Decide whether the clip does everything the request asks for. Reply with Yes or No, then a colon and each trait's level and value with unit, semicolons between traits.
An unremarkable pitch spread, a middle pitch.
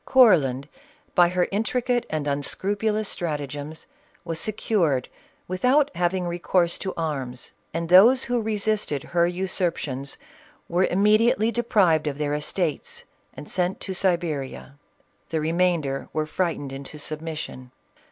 Yes: average, 5.0 semitones; medium, 175 Hz